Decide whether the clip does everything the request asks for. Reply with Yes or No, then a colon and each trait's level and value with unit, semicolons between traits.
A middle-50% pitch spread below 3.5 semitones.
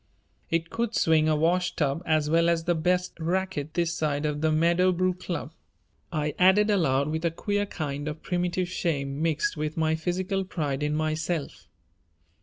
Yes: average, 2.8 semitones